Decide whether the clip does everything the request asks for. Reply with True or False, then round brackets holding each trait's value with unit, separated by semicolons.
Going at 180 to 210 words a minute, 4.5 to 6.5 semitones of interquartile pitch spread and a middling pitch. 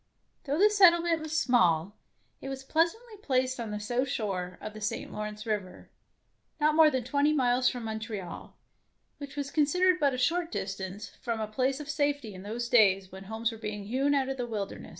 False (200 wpm; 5.5 semitones; 250 Hz)